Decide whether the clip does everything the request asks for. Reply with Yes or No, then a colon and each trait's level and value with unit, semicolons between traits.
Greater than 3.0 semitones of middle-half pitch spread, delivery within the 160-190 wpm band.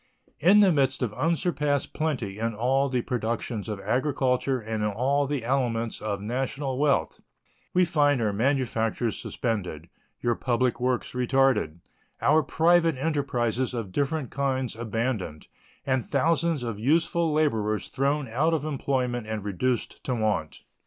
No: average, 4.2 semitones; average, 140 wpm